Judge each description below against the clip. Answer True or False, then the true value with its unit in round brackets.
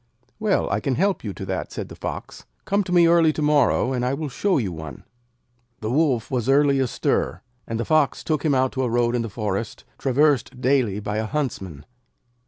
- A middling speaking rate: False (210 wpm)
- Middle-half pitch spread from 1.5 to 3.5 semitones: False (5.3 semitones)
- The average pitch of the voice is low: True (130 Hz)